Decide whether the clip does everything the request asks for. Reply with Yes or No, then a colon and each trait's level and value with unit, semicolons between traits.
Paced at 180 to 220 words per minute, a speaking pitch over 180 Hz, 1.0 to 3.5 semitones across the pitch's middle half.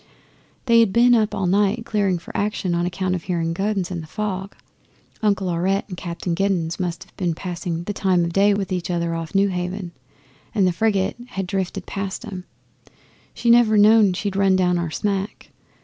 Yes: average, 190 wpm; high, 190 Hz; narrow, 2.5 semitones